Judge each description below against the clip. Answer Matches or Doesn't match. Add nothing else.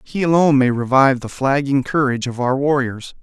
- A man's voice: Matches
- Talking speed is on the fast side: Doesn't match